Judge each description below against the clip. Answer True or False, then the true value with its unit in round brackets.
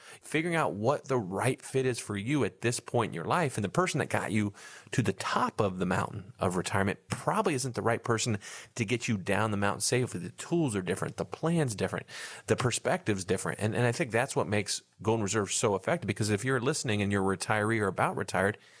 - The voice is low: True (110 Hz)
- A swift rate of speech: True (235 wpm)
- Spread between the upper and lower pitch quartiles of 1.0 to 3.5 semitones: False (4.1 semitones)